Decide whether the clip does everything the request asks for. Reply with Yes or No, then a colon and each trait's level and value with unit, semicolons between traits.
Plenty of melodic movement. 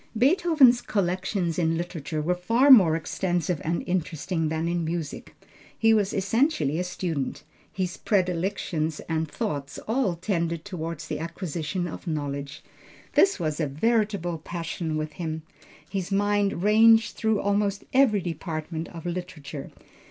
No: average, 4.2 semitones